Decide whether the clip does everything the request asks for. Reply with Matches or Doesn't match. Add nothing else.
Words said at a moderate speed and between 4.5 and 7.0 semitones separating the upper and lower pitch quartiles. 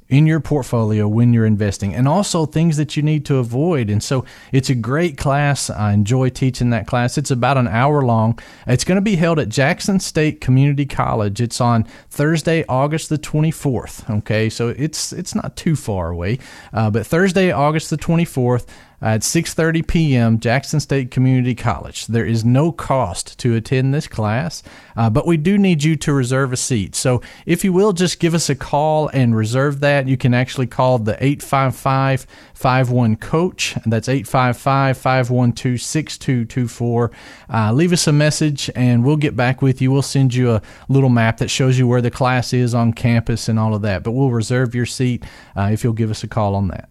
Doesn't match